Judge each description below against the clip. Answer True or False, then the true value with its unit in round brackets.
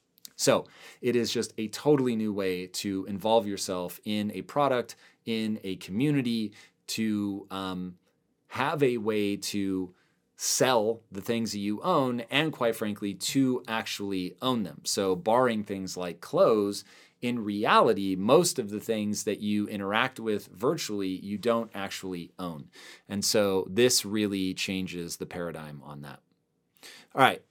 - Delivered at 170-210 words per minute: False (145 wpm)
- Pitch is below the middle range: True (105 Hz)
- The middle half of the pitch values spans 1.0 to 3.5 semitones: True (3.1 semitones)